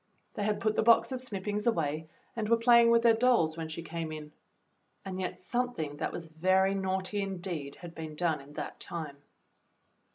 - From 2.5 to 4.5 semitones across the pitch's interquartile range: No, wide, 5.6 semitones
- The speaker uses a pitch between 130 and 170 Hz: No, medium, 185 Hz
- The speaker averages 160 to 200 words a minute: Yes, average, 190 wpm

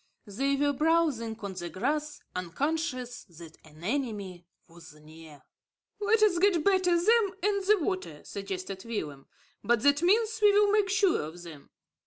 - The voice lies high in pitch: Yes, very high, 265 Hz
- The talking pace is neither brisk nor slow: Yes, average, 155 wpm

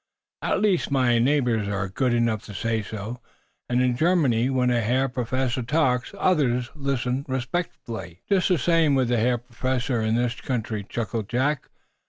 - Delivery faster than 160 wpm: Yes, average, 170 wpm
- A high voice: No, low, 125 Hz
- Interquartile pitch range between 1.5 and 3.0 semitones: Yes, average, 2.7 semitones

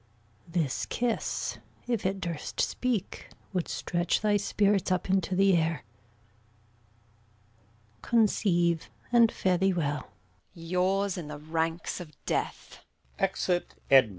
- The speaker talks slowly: Yes, slow, 120 wpm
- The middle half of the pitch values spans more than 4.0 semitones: No, average, 3.0 semitones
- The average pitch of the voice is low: No, medium, 180 Hz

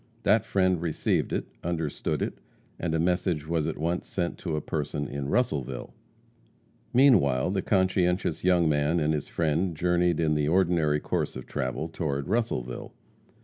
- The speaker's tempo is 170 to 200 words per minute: No, average, 155 wpm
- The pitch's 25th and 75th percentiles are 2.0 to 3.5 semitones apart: Yes, average, 3.2 semitones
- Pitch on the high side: No, very low, 80 Hz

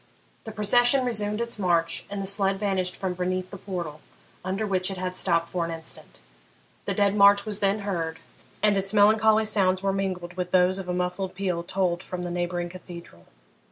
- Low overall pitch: No, high, 190 Hz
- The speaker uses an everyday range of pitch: No, narrow, 2.2 semitones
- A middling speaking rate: Yes, average, 190 wpm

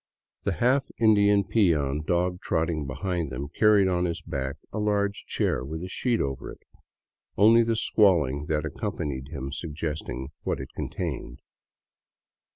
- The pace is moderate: Yes, average, 155 wpm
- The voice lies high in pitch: No, very low, 85 Hz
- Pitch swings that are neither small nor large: No, wide, 6.1 semitones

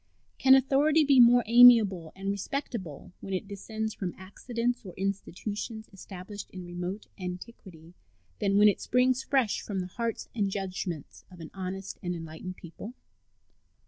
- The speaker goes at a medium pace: Yes, average, 145 wpm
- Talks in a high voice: Yes, high, 200 Hz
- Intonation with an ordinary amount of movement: Yes, average, 4.3 semitones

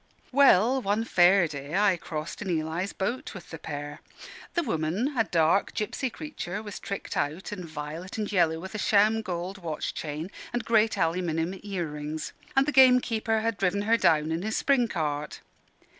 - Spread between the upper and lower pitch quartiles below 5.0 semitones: No, wide, 5.4 semitones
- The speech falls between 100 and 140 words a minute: No, average, 175 wpm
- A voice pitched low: No, high, 190 Hz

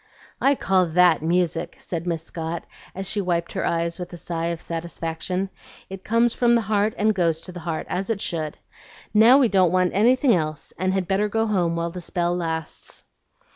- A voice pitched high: No, medium, 180 Hz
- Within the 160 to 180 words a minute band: No, average, 200 wpm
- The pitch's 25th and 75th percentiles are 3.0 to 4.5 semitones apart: Yes, average, 3.3 semitones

